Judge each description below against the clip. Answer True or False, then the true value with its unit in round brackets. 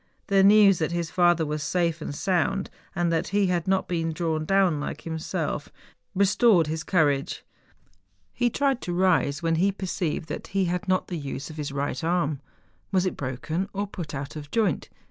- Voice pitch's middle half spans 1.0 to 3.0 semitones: False (3.6 semitones)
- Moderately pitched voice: True (175 Hz)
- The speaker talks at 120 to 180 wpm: False (200 wpm)